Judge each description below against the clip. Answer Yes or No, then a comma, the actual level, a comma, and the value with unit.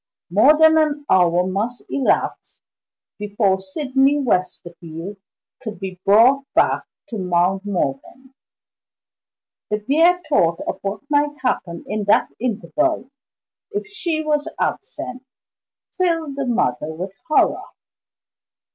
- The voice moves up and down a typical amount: No, wide, 7.7 semitones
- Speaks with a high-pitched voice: Yes, high, 230 Hz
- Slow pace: Yes, slow, 110 wpm